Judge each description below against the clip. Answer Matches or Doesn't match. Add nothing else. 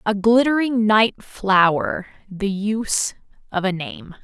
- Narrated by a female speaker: Matches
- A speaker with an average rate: Doesn't match